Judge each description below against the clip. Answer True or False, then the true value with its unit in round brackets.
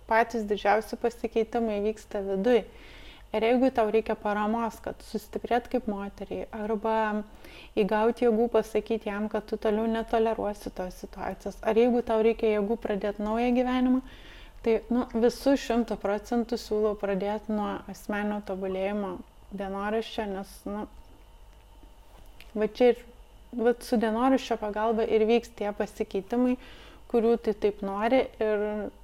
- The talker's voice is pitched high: True (220 Hz)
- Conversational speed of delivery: False (120 wpm)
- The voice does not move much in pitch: True (2.1 semitones)